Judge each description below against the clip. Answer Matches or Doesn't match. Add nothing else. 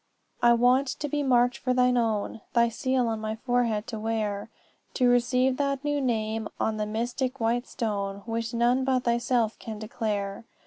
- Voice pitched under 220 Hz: Doesn't match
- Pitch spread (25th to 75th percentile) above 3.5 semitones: Doesn't match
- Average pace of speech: Matches